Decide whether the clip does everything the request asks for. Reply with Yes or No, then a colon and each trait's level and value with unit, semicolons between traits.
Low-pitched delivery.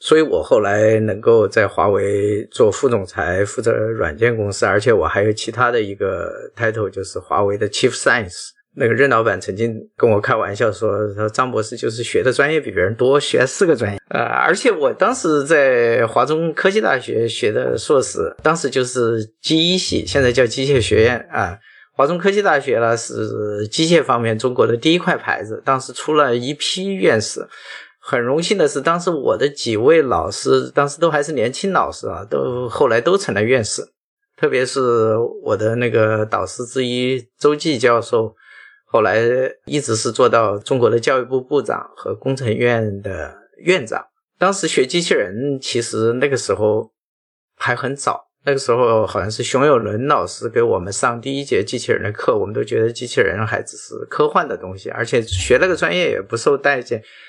No: medium, 150 Hz